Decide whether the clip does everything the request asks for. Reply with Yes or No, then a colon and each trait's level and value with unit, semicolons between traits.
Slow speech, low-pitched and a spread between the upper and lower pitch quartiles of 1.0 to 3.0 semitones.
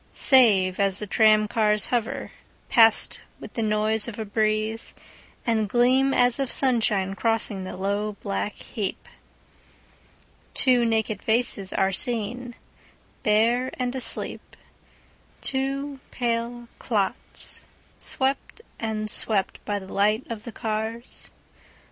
No: slow, 105 wpm; high, 220 Hz; narrow, 2.5 semitones